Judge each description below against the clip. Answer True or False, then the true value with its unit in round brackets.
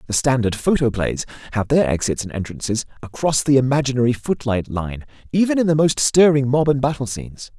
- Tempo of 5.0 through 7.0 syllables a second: True (5.7 syllables/s)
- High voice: False (130 Hz)